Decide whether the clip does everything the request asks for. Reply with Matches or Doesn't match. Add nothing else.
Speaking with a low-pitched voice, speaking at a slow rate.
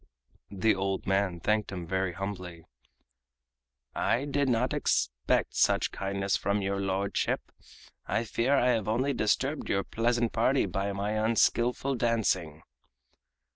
Matches